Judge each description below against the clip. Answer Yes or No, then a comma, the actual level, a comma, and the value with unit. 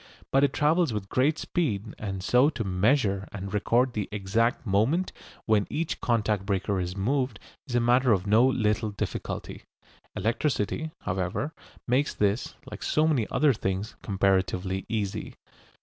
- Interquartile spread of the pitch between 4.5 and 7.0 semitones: Yes, average, 4.9 semitones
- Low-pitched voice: Yes, low, 110 Hz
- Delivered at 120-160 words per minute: Yes, average, 150 wpm